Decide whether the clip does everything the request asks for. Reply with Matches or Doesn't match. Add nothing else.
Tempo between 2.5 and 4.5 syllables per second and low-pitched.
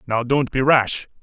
Matches